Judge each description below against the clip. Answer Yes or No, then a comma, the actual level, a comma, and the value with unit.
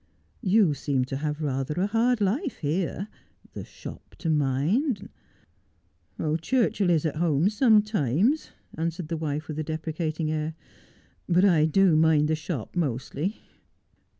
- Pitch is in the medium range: Yes, medium, 160 Hz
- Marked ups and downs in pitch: No, average, 4.4 semitones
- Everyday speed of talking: Yes, average, 150 wpm